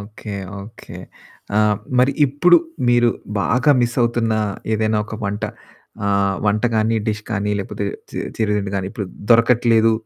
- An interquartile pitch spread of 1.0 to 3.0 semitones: Yes, narrow, 2.4 semitones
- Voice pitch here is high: No, low, 110 Hz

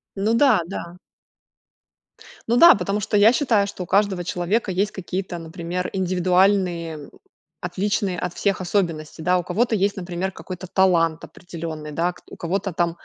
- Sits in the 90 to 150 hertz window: No, medium, 185 Hz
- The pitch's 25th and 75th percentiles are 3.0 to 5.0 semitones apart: No, narrow, 2.6 semitones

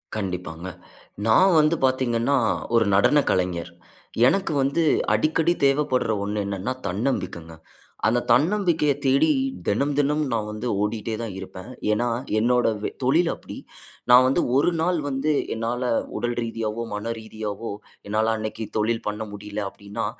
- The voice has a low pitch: Yes, low, 115 Hz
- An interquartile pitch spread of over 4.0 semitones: Yes, average, 4.8 semitones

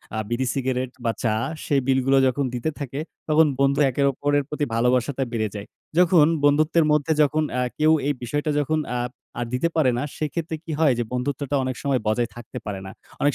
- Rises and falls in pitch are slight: No, average, 3.2 semitones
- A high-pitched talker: No, medium, 140 Hz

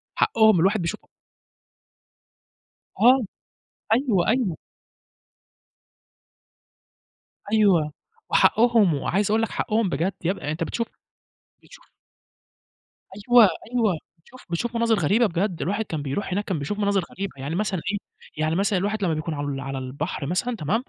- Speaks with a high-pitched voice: Yes, high, 195 Hz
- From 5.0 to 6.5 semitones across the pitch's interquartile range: Yes, average, 5.3 semitones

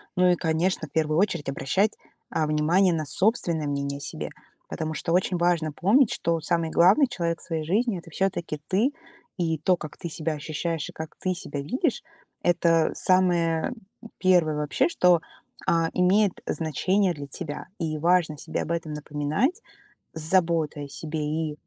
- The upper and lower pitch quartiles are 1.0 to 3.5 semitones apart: Yes, average, 3.0 semitones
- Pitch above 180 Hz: No, medium, 165 Hz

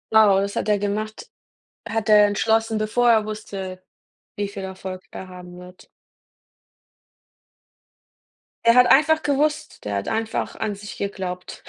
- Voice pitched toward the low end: No, high, 205 Hz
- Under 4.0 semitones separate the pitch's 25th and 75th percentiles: Yes, average, 2.8 semitones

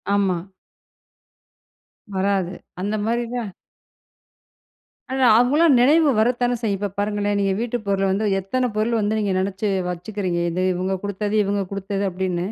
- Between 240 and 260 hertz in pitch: No, high, 205 Hz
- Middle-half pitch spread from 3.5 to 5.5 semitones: No, average, 2.9 semitones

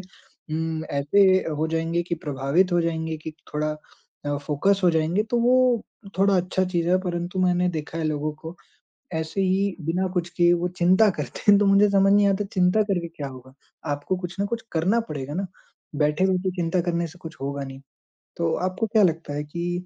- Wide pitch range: No, average, 3.3 semitones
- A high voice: No, medium, 175 Hz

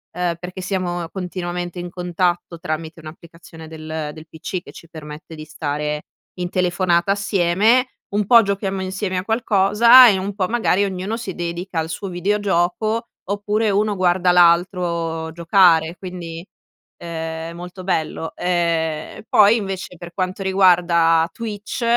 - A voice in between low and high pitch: Yes, medium, 180 Hz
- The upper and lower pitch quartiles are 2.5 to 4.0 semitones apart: Yes, average, 2.8 semitones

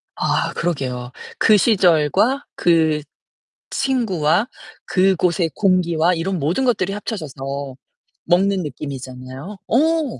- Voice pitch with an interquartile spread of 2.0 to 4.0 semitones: No, average, 5.3 semitones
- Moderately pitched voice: Yes, medium, 175 Hz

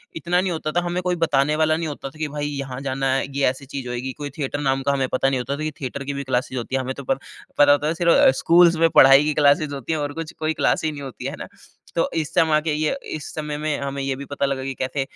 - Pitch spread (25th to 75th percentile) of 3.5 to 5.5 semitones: No, narrow, 2.4 semitones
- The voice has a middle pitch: Yes, medium, 145 Hz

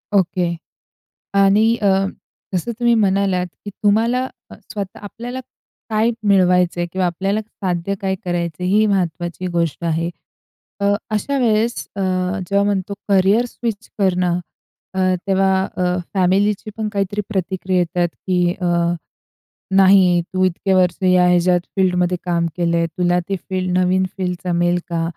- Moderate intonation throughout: No, narrow, 2.1 semitones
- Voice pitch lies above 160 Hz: Yes, medium, 185 Hz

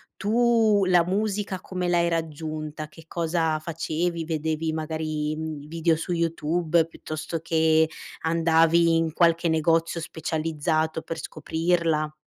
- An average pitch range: No, narrow, 1.4 semitones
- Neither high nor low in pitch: Yes, medium, 165 Hz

